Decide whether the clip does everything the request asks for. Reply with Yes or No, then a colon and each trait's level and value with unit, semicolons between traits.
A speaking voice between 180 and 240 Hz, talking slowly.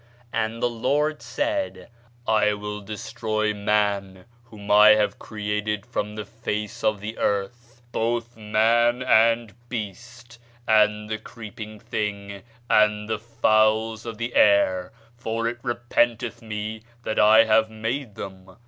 No: low, 110 Hz; slow, 130 wpm